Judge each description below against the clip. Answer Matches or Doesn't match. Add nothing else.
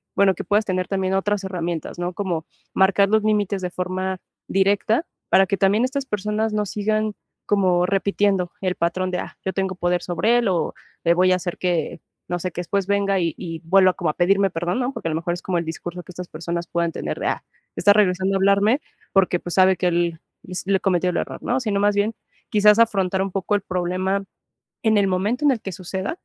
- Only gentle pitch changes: Matches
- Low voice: Doesn't match